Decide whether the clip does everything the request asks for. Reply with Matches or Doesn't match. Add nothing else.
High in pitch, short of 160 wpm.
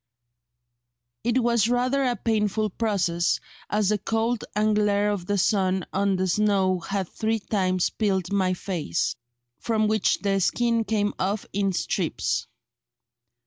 Matches